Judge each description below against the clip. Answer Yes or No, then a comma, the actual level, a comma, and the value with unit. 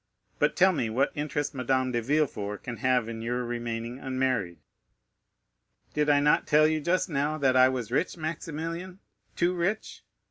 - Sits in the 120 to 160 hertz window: Yes, low, 135 Hz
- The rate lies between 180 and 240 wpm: No, average, 155 wpm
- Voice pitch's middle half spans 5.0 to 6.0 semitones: No, average, 4.3 semitones